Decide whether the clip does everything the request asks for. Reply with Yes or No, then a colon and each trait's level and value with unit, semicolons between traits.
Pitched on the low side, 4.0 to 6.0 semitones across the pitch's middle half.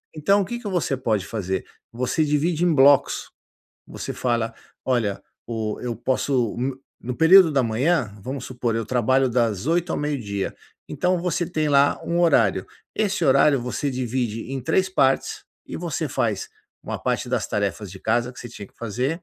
Yes: low, 130 Hz; average, 5.2 semitones